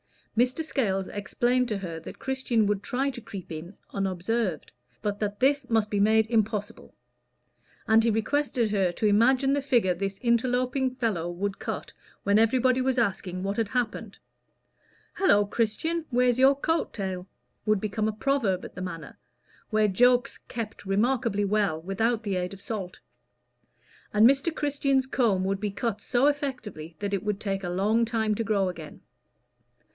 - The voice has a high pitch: Yes, high, 215 Hz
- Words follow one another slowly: No, average, 165 wpm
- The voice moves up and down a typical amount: Yes, average, 4.2 semitones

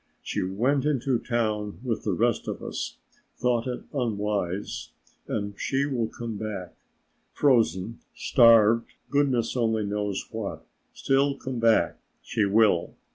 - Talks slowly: Yes, slow, 130 wpm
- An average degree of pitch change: Yes, average, 3.3 semitones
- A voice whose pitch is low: Yes, low, 115 Hz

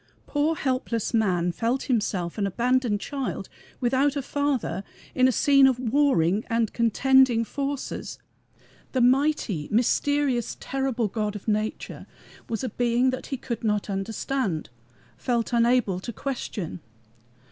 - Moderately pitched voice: No, high, 240 Hz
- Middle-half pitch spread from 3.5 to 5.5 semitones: Yes, average, 4.0 semitones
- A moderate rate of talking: No, slow, 130 wpm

